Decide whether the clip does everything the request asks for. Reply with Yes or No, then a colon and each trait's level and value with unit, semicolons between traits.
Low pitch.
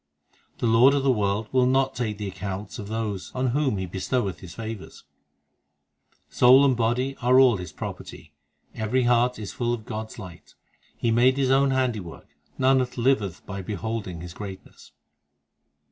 Yes: low, 115 Hz